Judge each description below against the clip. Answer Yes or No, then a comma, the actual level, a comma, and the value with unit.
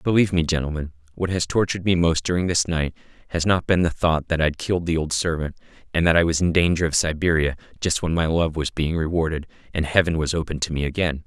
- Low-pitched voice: Yes, very low, 85 Hz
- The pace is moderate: No, fast, 235 wpm